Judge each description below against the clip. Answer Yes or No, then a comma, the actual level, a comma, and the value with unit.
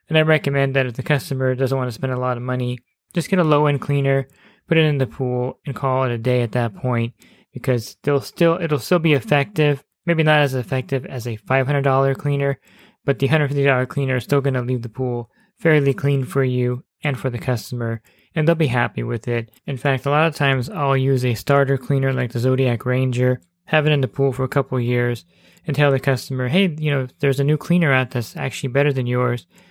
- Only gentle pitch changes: Yes, narrow, 2.3 semitones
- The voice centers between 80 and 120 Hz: No, low, 135 Hz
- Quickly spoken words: Yes, fast, 230 wpm